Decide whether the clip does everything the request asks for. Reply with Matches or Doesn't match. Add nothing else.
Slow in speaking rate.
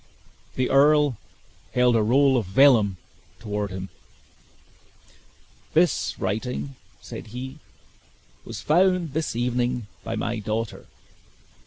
Matches